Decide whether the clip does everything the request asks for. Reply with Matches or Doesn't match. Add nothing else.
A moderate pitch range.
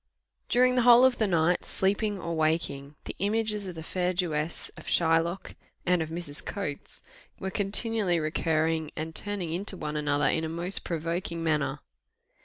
Matches